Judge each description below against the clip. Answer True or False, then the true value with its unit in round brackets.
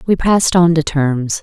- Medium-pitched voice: True (160 Hz)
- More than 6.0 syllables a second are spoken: False (4.7 syllables/s)